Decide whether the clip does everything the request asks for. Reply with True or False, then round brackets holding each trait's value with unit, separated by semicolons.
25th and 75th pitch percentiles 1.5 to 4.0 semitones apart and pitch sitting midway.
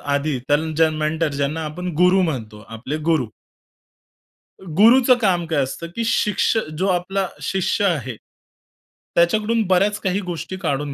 False (4.6 semitones; 170 Hz)